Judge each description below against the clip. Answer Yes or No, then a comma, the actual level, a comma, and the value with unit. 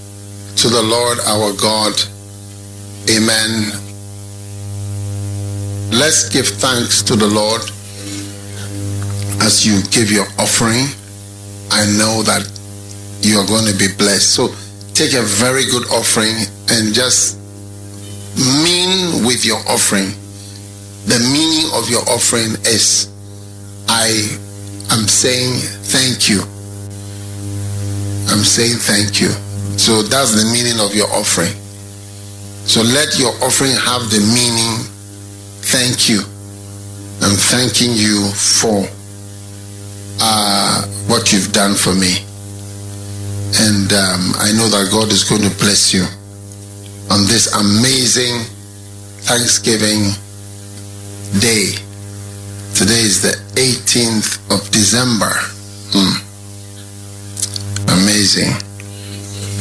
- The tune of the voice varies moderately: No, narrow, 1.6 semitones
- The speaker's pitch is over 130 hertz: No, low, 100 Hz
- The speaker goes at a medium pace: No, slow, 105 wpm